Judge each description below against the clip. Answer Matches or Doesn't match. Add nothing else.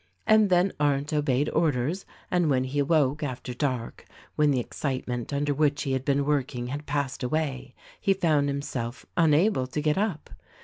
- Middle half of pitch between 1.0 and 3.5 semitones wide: Matches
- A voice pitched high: Doesn't match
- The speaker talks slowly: Doesn't match